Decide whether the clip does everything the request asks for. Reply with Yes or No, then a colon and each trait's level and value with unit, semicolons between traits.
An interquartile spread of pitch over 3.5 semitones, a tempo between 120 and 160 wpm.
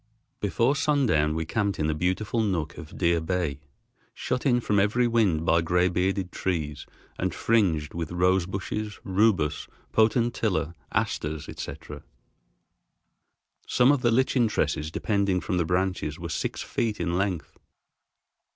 Yes: average, 5.1 semitones; average, 140 wpm